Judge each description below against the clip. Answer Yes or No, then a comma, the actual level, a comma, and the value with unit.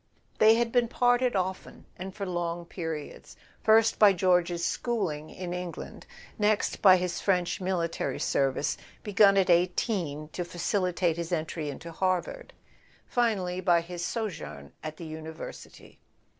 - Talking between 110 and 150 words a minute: Yes, slow, 135 wpm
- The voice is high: No, medium, 180 Hz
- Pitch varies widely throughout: No, average, 3.1 semitones